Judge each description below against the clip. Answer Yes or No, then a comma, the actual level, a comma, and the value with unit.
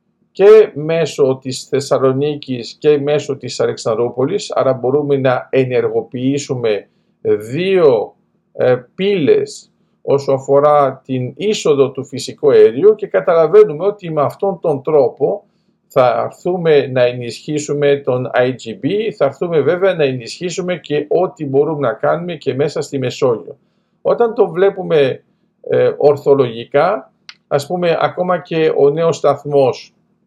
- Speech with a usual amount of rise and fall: No, wide, 7.0 semitones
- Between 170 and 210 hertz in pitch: No, medium, 160 Hz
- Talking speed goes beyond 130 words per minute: No, average, 120 wpm